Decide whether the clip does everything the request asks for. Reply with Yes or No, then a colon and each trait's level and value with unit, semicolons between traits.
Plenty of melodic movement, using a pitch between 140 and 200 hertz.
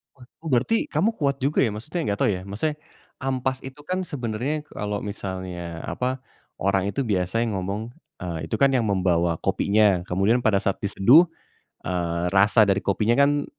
No: wide, 5.7 semitones; low, 105 Hz